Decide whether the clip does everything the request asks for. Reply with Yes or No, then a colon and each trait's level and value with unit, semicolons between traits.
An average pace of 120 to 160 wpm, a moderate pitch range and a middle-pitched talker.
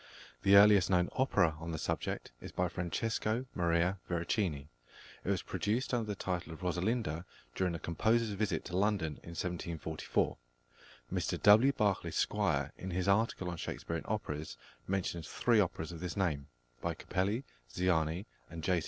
No: average, 155 wpm; average, 3.8 semitones; very low, 90 Hz